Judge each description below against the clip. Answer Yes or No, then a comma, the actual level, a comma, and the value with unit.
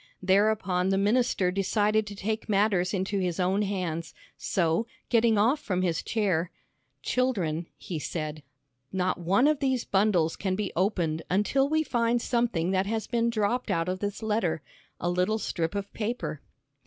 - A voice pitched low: No, high, 200 Hz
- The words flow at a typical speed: Yes, average, 160 wpm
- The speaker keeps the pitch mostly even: No, average, 3.6 semitones